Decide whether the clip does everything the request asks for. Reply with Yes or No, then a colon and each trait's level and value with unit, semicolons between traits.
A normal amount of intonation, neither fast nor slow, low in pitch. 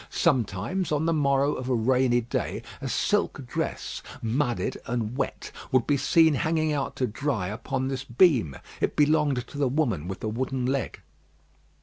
Yes: average, 3.7 semitones; average, 165 wpm; low, 130 Hz